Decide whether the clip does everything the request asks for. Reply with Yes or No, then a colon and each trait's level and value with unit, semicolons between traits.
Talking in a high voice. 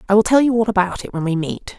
Yes: high, 200 Hz